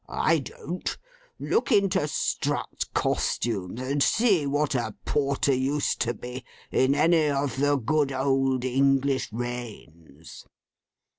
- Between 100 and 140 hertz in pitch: Yes, low, 135 Hz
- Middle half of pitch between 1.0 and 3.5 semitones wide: Yes, average, 3.0 semitones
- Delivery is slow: Yes, slow, 120 wpm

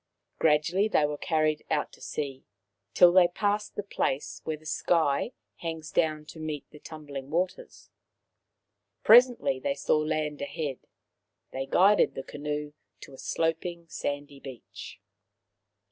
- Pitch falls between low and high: Yes, medium, 155 Hz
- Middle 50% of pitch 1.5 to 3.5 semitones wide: Yes, average, 2.9 semitones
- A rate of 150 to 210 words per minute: No, slow, 135 wpm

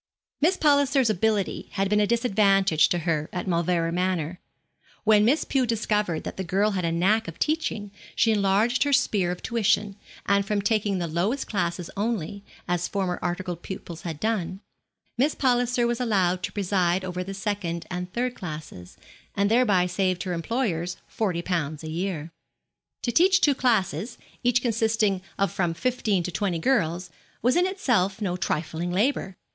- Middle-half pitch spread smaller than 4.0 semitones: No, average, 4.4 semitones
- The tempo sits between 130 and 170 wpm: Yes, average, 165 wpm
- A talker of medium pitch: No, high, 195 Hz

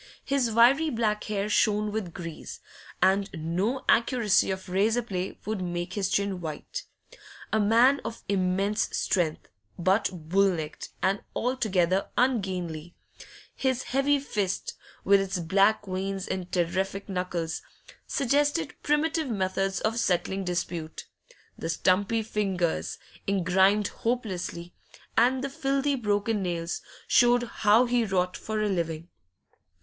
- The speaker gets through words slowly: Yes, slow, 125 wpm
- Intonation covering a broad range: No, average, 4.2 semitones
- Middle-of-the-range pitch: No, high, 200 Hz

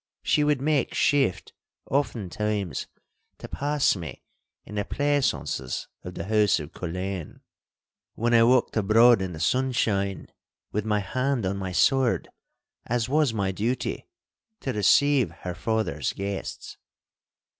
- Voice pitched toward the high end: No, low, 110 Hz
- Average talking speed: No, slow, 125 wpm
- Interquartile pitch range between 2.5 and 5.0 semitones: No, wide, 5.5 semitones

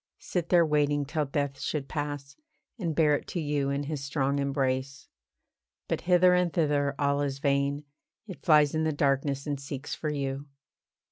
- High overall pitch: No, medium, 145 Hz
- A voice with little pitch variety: Yes, narrow, 1.7 semitones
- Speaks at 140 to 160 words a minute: No, average, 175 wpm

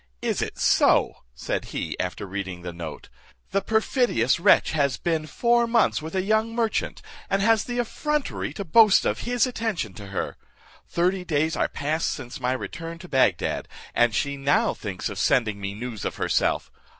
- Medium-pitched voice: Yes, medium, 160 Hz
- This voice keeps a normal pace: Yes, average, 175 wpm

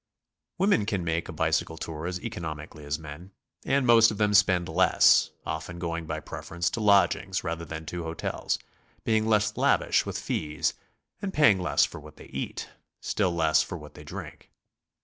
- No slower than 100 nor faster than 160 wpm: No, average, 175 wpm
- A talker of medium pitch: No, very low, 85 Hz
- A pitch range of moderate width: Yes, average, 4.5 semitones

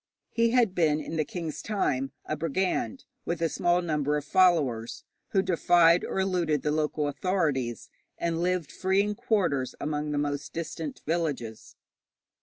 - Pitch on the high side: No, medium, 165 Hz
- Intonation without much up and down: No, average, 3.8 semitones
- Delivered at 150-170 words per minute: Yes, average, 155 wpm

